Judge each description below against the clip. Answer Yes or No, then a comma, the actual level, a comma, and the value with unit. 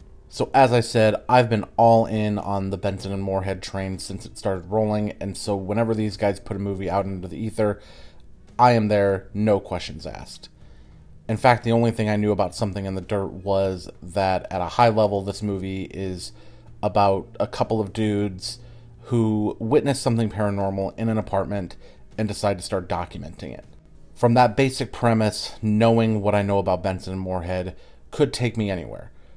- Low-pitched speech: Yes, low, 100 Hz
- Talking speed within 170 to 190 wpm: Yes, average, 185 wpm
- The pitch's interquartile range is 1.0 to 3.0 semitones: Yes, narrow, 2.6 semitones